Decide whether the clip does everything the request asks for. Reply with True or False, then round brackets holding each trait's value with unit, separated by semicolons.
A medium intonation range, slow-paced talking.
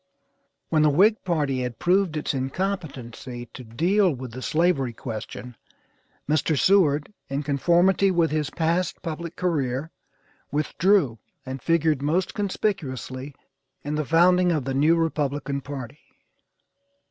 True (4.6 semitones; 125 wpm)